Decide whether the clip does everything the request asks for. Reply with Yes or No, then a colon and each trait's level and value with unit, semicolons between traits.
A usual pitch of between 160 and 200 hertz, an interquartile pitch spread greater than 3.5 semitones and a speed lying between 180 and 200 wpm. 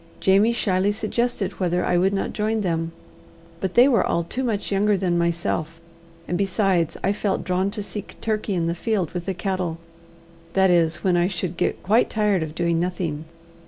No: medium, 185 Hz; average, 3.2 semitones; average, 190 wpm